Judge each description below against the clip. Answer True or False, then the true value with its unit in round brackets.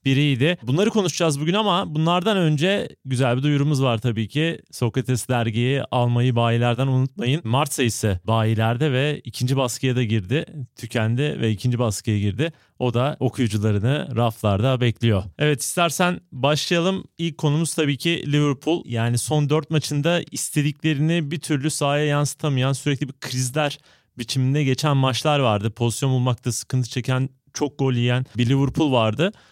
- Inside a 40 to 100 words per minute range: False (140 wpm)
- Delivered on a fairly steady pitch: False (3.8 semitones)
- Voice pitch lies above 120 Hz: True (135 Hz)